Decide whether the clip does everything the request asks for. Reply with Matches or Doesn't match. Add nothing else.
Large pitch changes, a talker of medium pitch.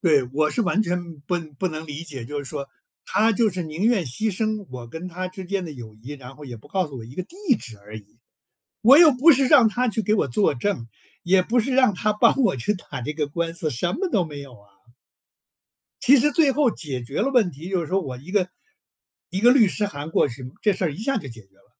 Matches